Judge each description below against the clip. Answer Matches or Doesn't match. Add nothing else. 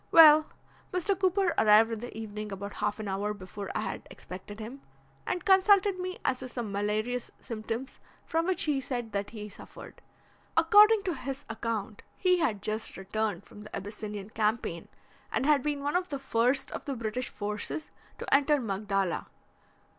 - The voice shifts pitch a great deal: Matches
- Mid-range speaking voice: Doesn't match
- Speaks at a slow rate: Doesn't match